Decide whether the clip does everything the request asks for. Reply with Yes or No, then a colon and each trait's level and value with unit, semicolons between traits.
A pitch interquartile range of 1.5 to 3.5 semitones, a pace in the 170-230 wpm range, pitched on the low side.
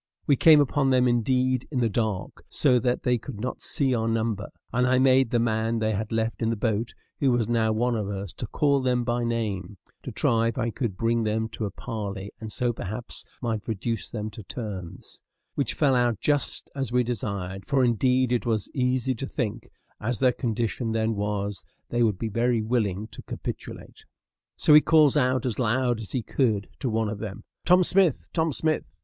Yes: average, 2.8 semitones; fast, 205 wpm; low, 115 Hz